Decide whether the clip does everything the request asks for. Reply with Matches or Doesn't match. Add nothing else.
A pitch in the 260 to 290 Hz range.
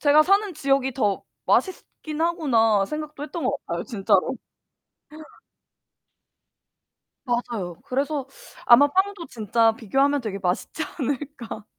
Matches